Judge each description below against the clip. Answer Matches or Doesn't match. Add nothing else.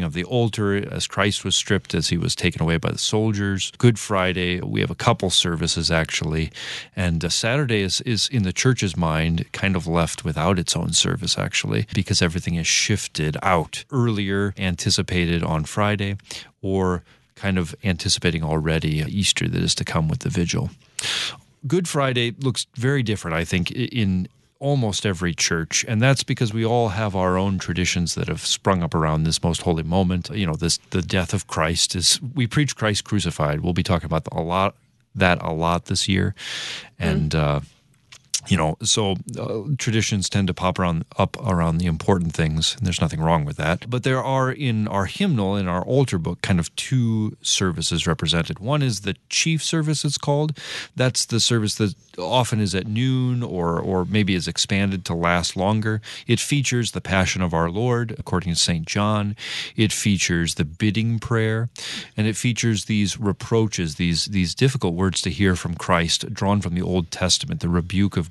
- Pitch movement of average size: Matches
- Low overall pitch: Matches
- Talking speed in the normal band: Matches